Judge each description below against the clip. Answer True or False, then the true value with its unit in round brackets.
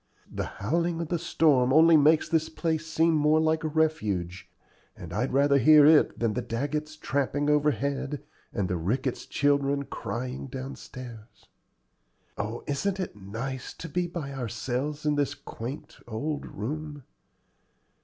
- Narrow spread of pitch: False (3.8 semitones)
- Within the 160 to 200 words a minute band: False (145 wpm)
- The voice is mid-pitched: True (145 Hz)